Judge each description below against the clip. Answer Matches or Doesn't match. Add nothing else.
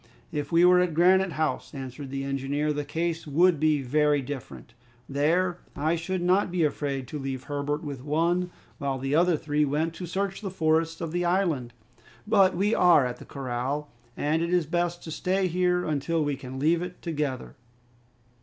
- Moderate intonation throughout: Matches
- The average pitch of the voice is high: Doesn't match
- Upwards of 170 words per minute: Matches